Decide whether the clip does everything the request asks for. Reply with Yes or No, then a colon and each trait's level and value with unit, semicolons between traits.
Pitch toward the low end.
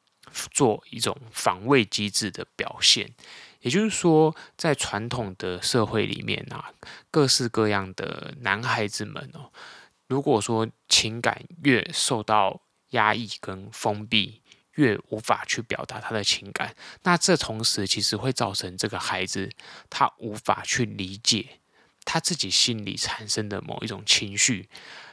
Yes: low, 110 Hz